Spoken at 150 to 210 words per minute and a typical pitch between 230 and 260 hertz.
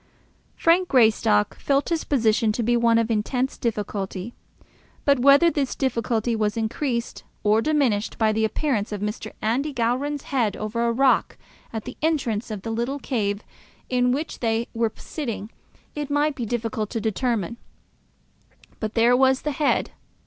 Yes: average, 155 wpm; high, 235 Hz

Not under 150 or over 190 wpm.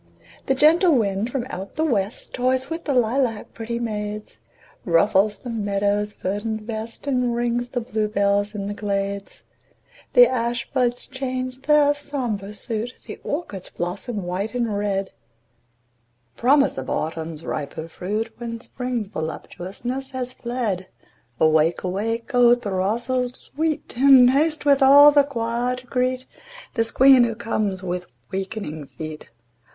No: slow, 135 wpm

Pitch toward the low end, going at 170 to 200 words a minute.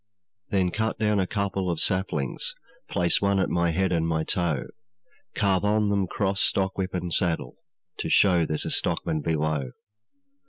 No: very low, 90 Hz; average, 160 wpm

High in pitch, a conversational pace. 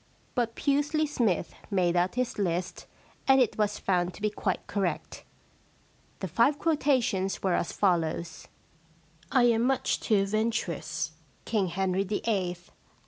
Yes: high, 195 Hz; average, 160 wpm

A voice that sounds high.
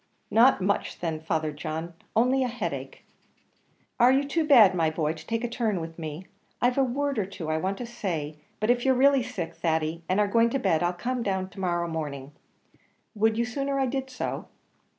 Yes: high, 205 Hz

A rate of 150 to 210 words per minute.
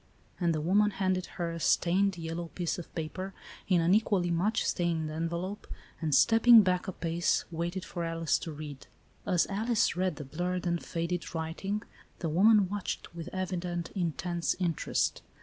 Yes: average, 165 wpm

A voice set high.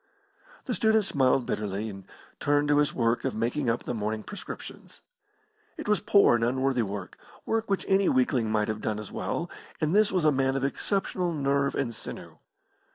No: low, 135 Hz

